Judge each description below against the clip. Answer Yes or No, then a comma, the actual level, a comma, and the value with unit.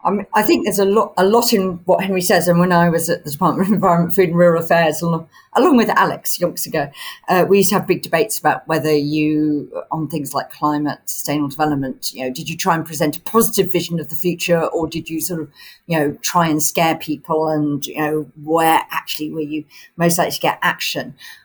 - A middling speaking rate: No, fast, 225 wpm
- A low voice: No, medium, 165 Hz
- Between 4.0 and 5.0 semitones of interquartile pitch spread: No, average, 2.8 semitones